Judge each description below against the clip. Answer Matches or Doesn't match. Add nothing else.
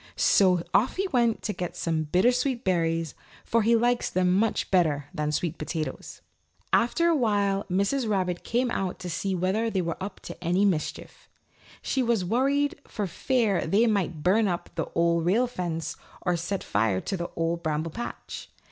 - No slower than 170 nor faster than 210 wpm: Matches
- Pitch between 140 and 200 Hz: Matches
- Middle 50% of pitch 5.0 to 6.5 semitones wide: Matches